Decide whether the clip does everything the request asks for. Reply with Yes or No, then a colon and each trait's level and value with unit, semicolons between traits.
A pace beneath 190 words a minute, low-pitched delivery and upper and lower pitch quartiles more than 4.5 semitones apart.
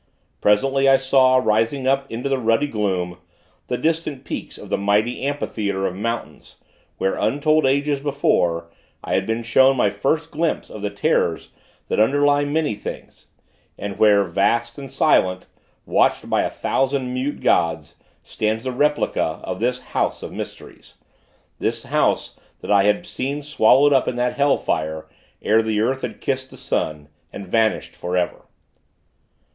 Yes: average, 160 wpm; low, 125 Hz; average, 5.1 semitones